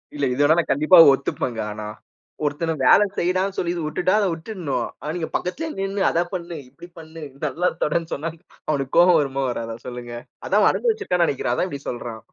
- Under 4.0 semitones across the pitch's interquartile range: No, average, 4.7 semitones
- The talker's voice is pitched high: No, medium, 160 Hz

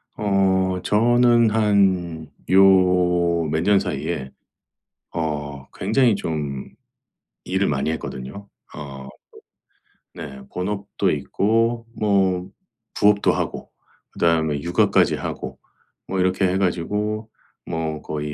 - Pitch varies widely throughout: No, average, 4.3 semitones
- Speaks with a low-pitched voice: Yes, very low, 90 Hz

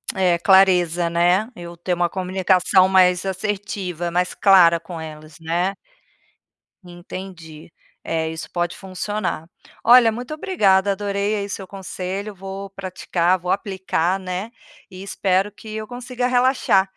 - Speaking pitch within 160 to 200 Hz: Yes, high, 190 Hz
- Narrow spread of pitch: Yes, narrow, 2.3 semitones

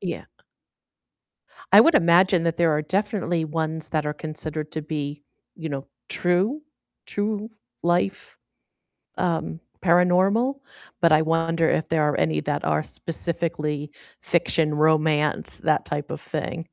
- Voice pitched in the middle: Yes, medium, 160 Hz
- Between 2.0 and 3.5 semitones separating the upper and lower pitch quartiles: Yes, narrow, 2.5 semitones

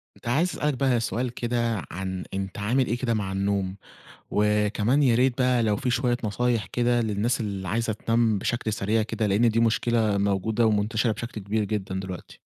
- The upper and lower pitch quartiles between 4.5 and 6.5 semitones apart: No, average, 2.8 semitones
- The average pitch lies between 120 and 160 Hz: No, low, 110 Hz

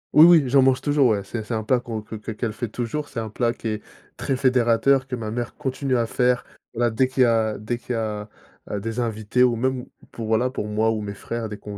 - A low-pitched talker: Yes, low, 120 Hz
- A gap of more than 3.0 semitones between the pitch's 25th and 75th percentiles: No, average, 2.7 semitones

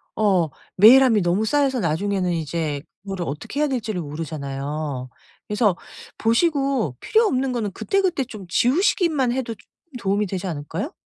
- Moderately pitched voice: No, high, 205 Hz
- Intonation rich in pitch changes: Yes, wide, 7.9 semitones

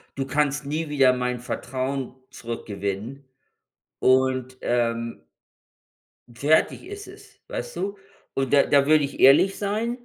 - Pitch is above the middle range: No, low, 135 Hz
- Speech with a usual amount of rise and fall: Yes, average, 3.5 semitones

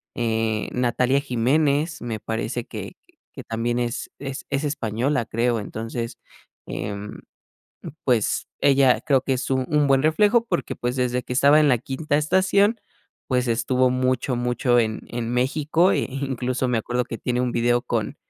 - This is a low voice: Yes, low, 125 Hz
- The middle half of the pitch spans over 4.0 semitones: No, average, 2.9 semitones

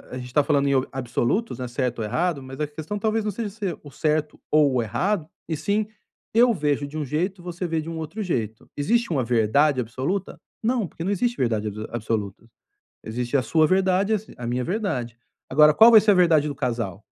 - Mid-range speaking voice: Yes, medium, 150 Hz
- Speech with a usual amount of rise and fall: No, wide, 7.6 semitones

